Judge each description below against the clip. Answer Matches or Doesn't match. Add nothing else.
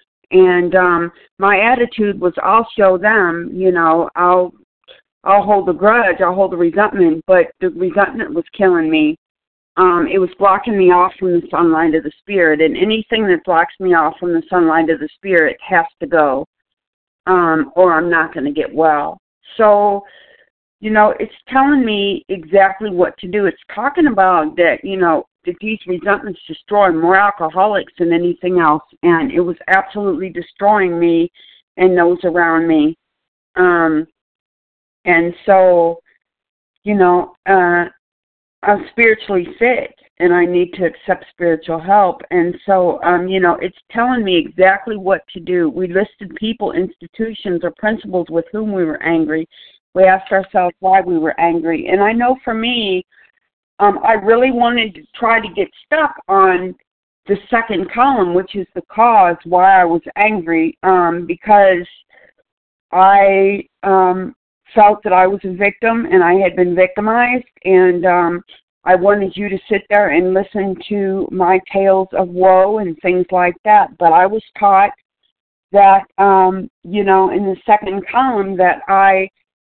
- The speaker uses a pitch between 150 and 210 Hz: Matches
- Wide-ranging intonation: Doesn't match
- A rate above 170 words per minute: Doesn't match